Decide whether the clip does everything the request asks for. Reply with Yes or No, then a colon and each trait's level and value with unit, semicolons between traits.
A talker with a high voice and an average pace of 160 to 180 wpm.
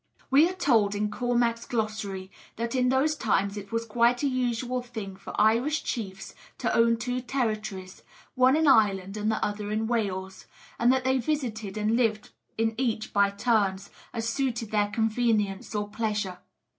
Yes: high, 225 Hz; average, 170 wpm